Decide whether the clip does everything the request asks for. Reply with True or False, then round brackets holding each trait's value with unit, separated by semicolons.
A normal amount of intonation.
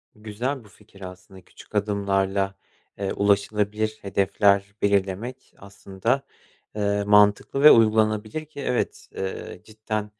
False (1.7 semitones)